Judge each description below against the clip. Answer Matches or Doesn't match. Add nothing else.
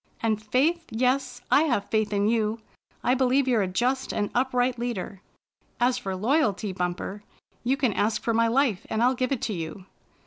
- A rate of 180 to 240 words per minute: Matches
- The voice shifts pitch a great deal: Doesn't match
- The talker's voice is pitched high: Matches